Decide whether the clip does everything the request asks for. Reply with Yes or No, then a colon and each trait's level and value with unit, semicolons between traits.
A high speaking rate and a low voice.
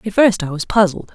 No: fast, 260 wpm; high, 195 Hz